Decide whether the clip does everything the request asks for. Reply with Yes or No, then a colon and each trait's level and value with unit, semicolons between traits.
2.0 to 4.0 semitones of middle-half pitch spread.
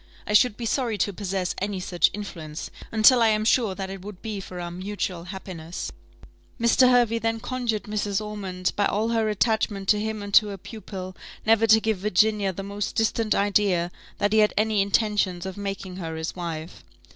Yes: average, 2.7 semitones